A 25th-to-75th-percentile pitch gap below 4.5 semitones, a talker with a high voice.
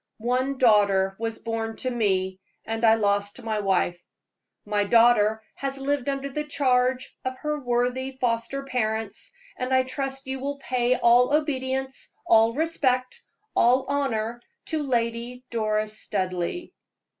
Yes: average, 3.3 semitones; high, 245 Hz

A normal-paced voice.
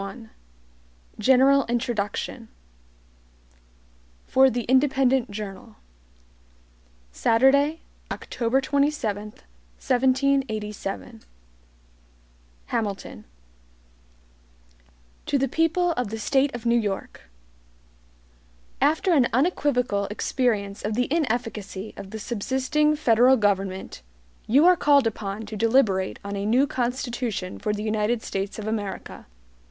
No: slow, 100 wpm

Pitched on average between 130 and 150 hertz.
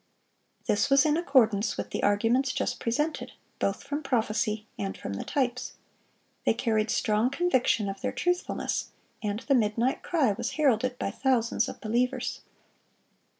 No: high, 240 Hz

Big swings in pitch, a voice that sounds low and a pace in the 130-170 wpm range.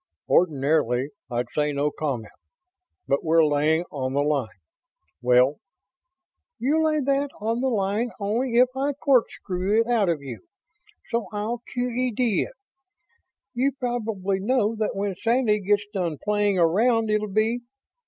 No: wide, 7.5 semitones; high, 210 Hz; average, 140 wpm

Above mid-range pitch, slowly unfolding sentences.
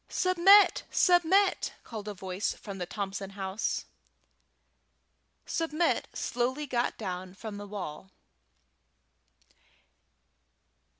Yes: high, 210 Hz; slow, 85 wpm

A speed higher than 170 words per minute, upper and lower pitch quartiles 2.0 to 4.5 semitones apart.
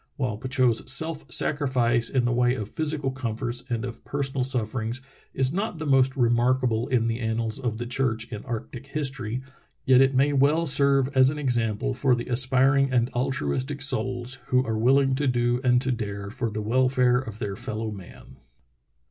Yes: average, 180 wpm; narrow, 2.4 semitones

